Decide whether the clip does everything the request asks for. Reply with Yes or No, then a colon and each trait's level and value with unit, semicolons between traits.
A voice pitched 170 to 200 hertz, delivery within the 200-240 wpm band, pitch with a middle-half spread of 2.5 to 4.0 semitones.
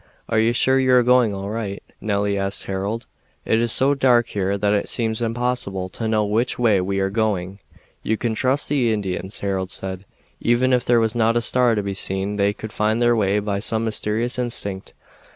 No: low, 110 Hz; fast, 205 wpm; average, 3.2 semitones